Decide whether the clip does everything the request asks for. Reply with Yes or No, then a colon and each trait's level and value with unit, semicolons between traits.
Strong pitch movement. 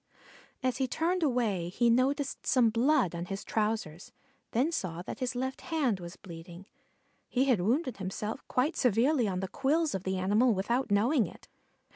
Yes: wide, 5.7 semitones